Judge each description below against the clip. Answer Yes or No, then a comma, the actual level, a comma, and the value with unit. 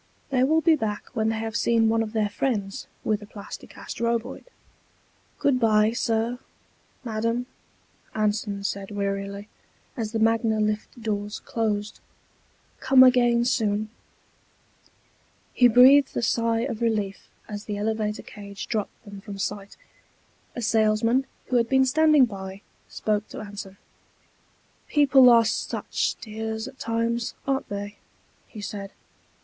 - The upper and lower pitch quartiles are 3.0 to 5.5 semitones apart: No, narrow, 2.4 semitones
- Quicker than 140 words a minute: No, slow, 135 wpm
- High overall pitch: Yes, high, 220 Hz